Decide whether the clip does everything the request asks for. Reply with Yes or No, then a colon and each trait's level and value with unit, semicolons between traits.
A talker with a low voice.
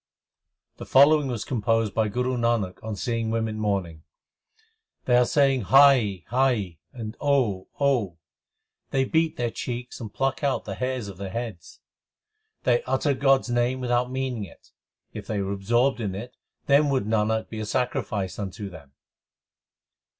Yes: low, 120 Hz